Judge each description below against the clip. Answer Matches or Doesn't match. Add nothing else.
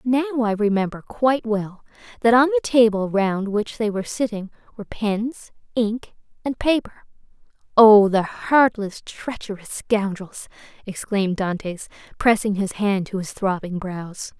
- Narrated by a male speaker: Doesn't match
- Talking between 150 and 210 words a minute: Doesn't match